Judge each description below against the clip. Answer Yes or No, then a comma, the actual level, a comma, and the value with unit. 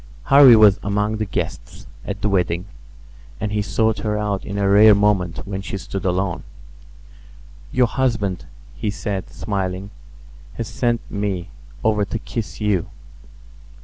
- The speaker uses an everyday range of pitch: No, narrow, 1.9 semitones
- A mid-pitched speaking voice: No, low, 105 Hz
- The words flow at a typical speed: Yes, average, 145 wpm